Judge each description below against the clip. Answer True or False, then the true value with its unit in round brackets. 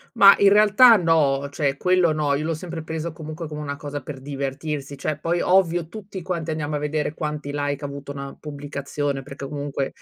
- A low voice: False (150 Hz)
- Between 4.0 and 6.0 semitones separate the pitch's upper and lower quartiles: False (2.8 semitones)